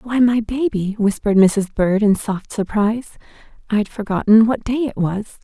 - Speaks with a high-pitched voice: Yes, high, 215 Hz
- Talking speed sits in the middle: Yes, average, 175 wpm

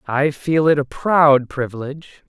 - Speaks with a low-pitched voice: No, medium, 145 Hz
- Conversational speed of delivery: Yes, average, 160 wpm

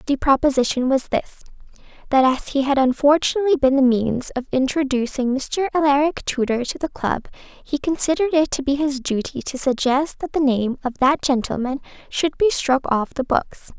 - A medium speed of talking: Yes, average, 180 wpm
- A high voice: Yes, very high, 275 Hz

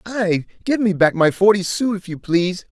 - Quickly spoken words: Yes, fast, 215 wpm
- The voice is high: Yes, high, 195 Hz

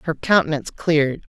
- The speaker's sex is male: No, female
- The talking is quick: No, slow, 135 wpm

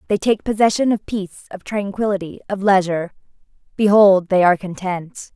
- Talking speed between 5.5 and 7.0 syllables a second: Yes, 5.7 syllables/s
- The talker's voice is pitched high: Yes, high, 195 Hz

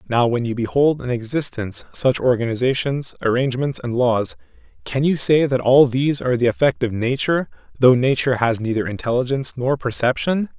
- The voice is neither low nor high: No, low, 125 Hz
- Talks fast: No, average, 165 wpm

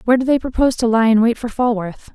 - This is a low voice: No, high, 235 Hz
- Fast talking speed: Yes, fast, 280 wpm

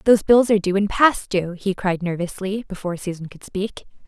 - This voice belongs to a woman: Yes, female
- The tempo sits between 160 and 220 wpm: Yes, fast, 205 wpm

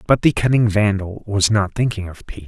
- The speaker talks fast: Yes, fast, 220 wpm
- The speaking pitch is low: Yes, low, 105 Hz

